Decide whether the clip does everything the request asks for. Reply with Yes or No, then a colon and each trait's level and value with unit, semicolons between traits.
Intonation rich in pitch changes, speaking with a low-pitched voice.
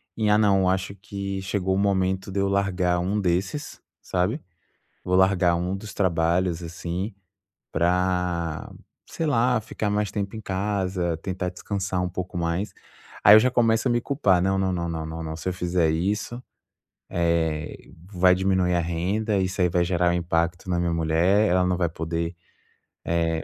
No: narrow, 2.4 semitones; very low, 90 Hz